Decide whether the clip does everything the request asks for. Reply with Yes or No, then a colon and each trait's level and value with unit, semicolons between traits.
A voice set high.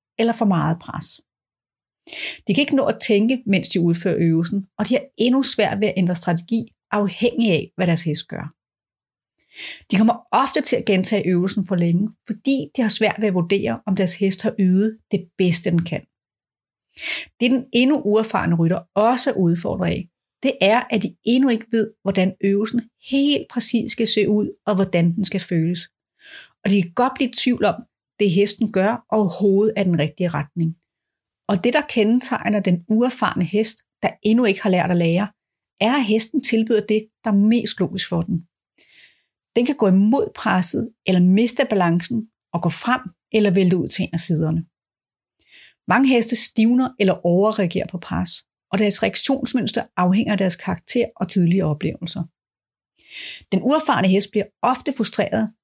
Yes: high, 205 Hz